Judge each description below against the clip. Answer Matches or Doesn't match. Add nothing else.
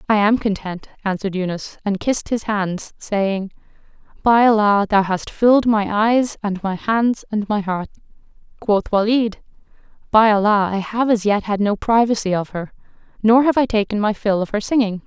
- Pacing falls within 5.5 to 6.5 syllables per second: Doesn't match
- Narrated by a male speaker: Doesn't match